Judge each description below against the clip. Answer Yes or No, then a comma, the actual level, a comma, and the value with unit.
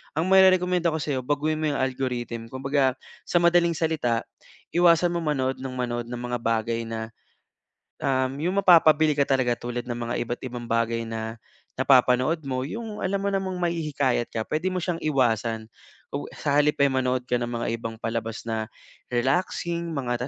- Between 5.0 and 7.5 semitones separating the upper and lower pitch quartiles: Yes, average, 5.3 semitones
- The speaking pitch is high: No, low, 130 Hz